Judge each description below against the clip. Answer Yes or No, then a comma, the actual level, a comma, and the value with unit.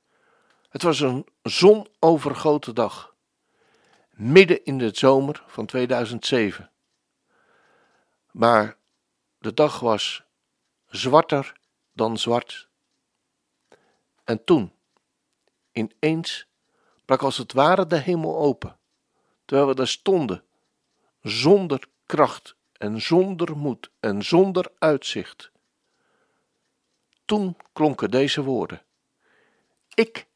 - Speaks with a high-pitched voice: No, medium, 145 Hz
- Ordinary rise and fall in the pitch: No, wide, 6.6 semitones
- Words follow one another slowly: Yes, slow, 90 wpm